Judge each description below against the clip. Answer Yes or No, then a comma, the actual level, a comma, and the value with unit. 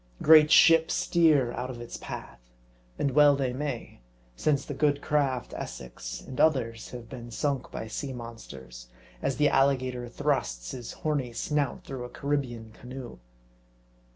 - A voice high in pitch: No, low, 130 Hz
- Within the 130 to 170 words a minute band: Yes, average, 150 wpm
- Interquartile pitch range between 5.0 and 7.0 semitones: No, average, 3.4 semitones